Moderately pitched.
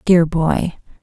Yes: medium, 170 Hz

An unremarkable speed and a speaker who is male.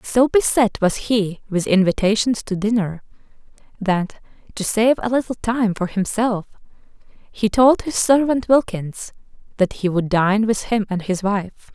No: average, 155 wpm; female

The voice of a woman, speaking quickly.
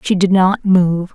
Yes: female; fast, 210 wpm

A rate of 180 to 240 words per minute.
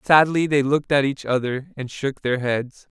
Yes: average, 200 wpm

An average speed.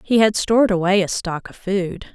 No: fast, 225 wpm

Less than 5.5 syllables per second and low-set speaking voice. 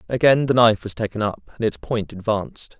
No: 5.8 syllables/s; low, 115 Hz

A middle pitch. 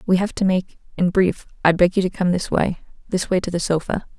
Yes: medium, 180 Hz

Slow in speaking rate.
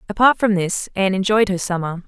No: average, 200 wpm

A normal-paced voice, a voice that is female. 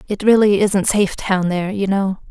No: fast, 210 wpm; female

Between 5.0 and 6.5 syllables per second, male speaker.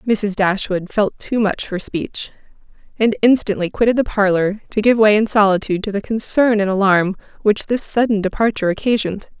No: 5.4 syllables/s; female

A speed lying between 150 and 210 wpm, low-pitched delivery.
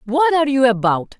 No: average, 200 wpm; very high, 260 Hz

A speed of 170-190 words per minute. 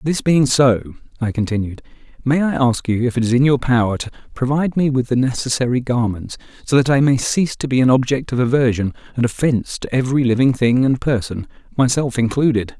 No: average, 200 wpm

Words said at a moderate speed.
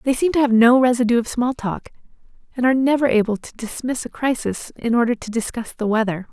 No: fast, 220 wpm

